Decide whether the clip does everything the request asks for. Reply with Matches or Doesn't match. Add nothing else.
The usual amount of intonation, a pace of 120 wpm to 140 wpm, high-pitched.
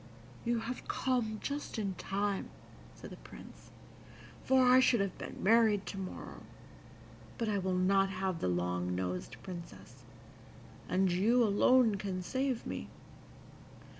Matches